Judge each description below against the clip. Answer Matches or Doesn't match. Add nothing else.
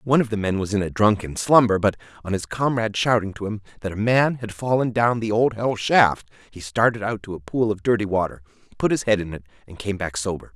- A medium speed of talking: Doesn't match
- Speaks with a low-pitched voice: Matches